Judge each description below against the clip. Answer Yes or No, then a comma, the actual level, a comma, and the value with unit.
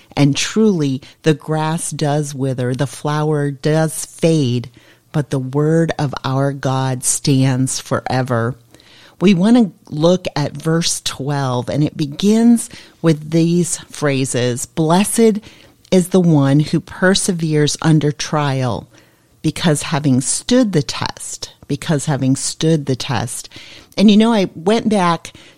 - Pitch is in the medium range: Yes, medium, 150 Hz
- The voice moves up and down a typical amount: Yes, average, 3.9 semitones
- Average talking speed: No, slow, 130 wpm